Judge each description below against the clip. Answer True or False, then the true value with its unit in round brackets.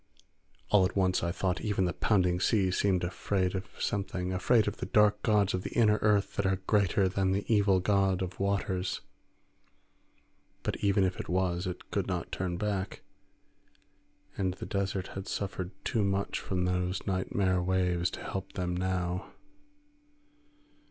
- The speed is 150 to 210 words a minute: True (160 wpm)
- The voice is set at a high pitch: False (95 Hz)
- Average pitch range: False (1.6 semitones)